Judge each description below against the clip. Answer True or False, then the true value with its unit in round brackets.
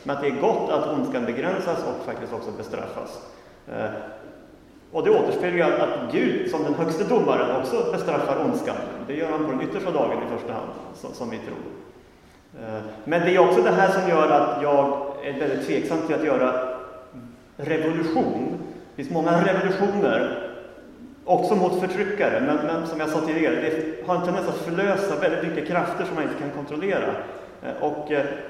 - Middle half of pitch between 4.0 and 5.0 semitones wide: True (4.6 semitones)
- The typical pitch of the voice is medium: True (165 Hz)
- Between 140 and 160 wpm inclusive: False (175 wpm)